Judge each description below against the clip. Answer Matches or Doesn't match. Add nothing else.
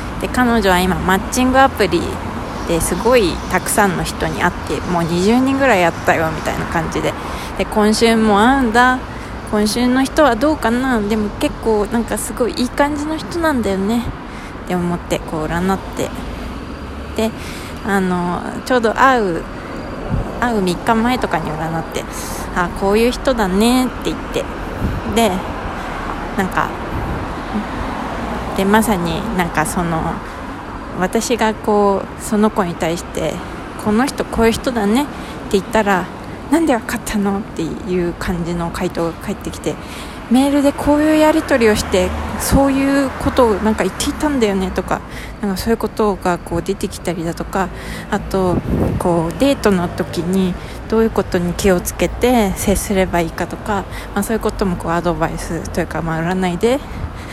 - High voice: Matches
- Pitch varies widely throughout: Doesn't match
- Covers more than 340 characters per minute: Doesn't match